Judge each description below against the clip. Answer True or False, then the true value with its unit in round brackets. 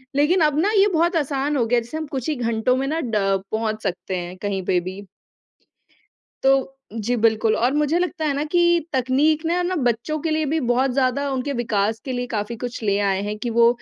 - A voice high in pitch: True (255 Hz)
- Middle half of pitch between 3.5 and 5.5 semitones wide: True (5.2 semitones)